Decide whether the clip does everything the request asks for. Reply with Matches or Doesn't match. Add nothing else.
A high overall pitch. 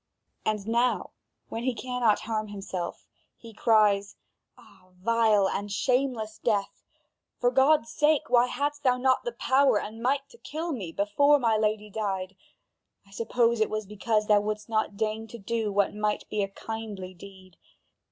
Matches